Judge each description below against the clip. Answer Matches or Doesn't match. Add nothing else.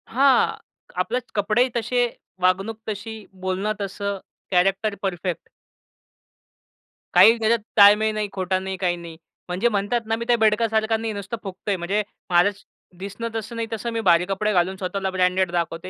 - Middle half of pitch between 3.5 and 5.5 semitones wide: Doesn't match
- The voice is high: Matches